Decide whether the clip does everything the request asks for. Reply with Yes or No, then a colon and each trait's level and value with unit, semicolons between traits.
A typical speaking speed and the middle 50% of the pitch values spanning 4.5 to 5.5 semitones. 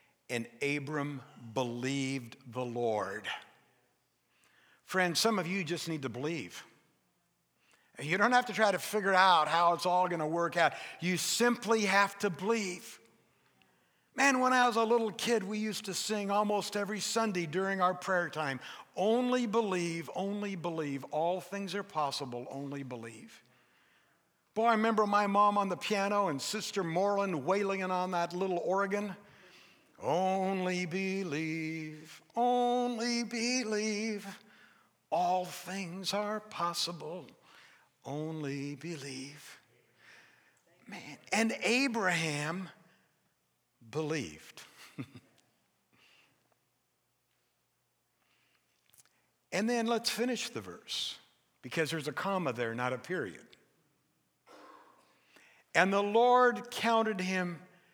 No: slow, 115 wpm; average, 5.2 semitones